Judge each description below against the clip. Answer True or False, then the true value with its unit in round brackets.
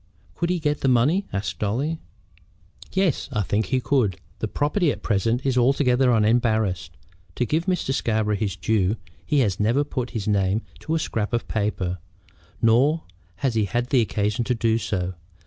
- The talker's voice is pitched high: False (115 Hz)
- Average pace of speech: True (170 wpm)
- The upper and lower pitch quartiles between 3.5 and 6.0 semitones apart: True (4.7 semitones)